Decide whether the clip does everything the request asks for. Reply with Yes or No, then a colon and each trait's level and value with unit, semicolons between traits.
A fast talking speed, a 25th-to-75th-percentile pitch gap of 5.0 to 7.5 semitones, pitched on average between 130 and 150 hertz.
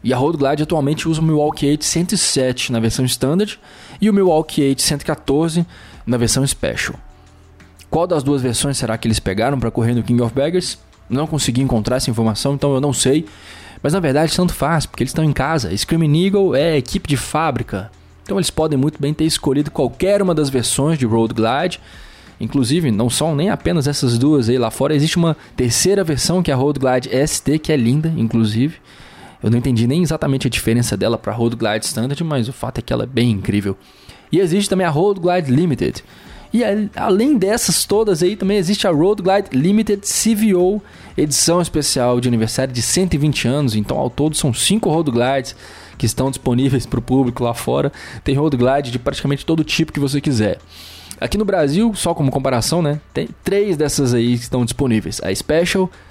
Yes: fast, 200 wpm; wide, 5.4 semitones; medium, 140 Hz